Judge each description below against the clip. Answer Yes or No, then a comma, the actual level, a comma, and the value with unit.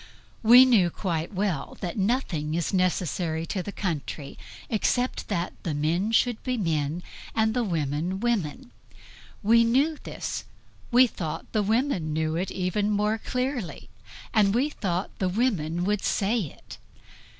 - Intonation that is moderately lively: No, wide, 5.7 semitones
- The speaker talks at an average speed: Yes, average, 145 wpm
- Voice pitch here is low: No, high, 195 Hz